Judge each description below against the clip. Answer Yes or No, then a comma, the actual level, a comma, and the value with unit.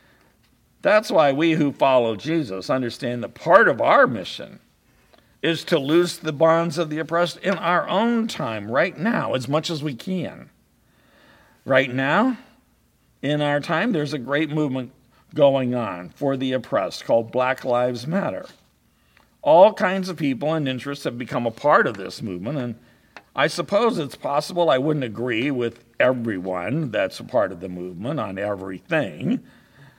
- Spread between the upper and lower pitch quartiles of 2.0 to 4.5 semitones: No, average, 5.1 semitones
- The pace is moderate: Yes, average, 160 wpm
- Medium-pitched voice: Yes, medium, 145 Hz